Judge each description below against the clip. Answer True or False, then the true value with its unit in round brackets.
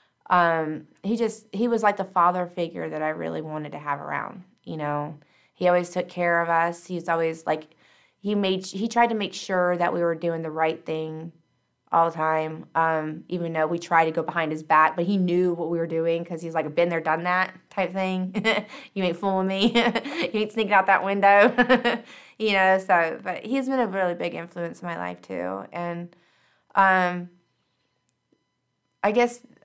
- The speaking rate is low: False (200 wpm)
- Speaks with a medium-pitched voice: True (175 Hz)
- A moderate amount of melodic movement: True (3.2 semitones)